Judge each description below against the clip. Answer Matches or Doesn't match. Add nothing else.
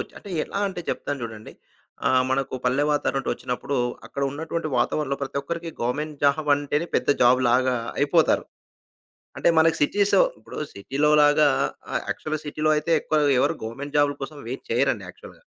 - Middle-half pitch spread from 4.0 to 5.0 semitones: Doesn't match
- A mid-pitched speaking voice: Matches